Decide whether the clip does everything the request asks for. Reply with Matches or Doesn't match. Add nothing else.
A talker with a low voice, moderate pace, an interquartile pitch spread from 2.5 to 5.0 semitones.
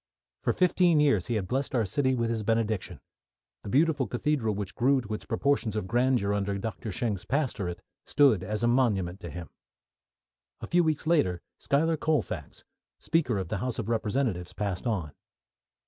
Doesn't match